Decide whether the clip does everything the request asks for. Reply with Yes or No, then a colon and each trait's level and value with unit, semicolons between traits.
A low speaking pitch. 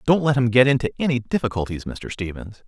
Yes: low, 120 Hz